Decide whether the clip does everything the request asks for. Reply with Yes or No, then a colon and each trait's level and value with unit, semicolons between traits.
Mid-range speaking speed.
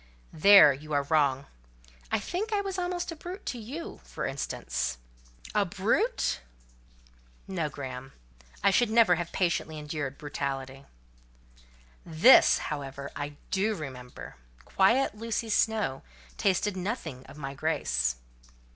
No: slow, 125 wpm